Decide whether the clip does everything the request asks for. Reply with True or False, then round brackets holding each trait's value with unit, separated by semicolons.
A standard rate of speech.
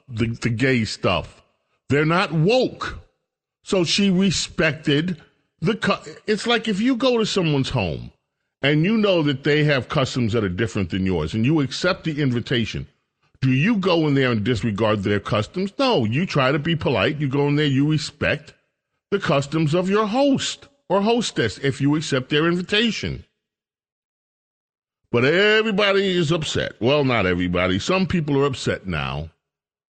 True (165 wpm)